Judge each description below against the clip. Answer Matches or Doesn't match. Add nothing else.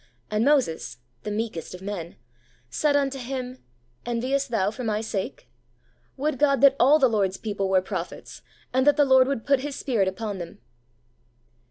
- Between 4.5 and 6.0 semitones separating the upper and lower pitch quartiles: Matches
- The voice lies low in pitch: Doesn't match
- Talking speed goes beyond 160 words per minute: Matches